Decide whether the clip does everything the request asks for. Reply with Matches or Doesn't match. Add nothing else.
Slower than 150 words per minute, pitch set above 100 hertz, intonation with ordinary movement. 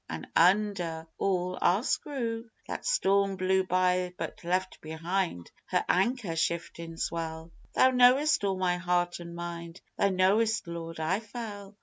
Matches